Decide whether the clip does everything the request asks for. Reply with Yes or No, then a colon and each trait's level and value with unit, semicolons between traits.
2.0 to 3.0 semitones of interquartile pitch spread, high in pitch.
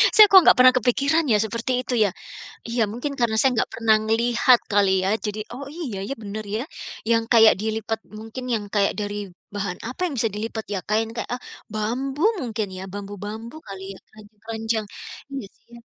Yes: average, 2.7 semitones; high, 225 Hz